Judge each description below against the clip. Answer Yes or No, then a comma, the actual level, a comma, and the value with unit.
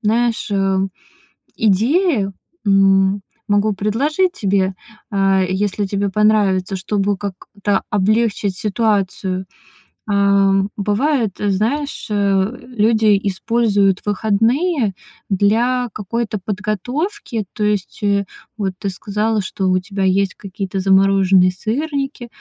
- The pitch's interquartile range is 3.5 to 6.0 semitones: No, narrow, 2.4 semitones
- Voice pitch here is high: Yes, high, 205 Hz